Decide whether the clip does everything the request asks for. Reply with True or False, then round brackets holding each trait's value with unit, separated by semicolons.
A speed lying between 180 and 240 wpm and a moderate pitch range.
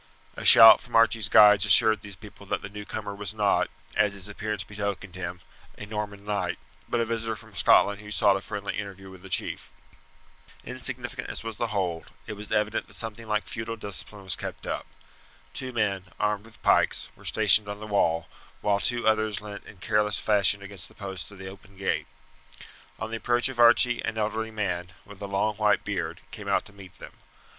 False (200 wpm; 1.7 semitones)